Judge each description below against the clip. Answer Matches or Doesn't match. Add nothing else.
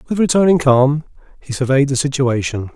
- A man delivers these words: Matches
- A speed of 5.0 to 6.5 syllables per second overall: Matches